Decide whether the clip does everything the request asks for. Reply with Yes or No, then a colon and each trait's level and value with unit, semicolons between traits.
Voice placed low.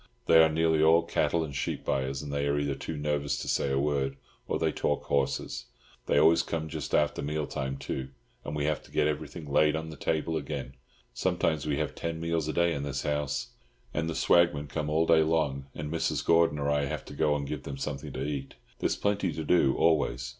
Yes: very low, 75 Hz